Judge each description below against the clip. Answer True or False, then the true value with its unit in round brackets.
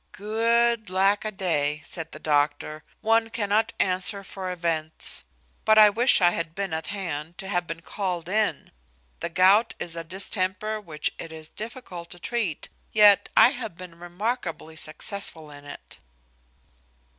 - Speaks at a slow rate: False (155 wpm)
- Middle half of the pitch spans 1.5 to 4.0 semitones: False (4.5 semitones)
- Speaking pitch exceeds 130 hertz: True (185 Hz)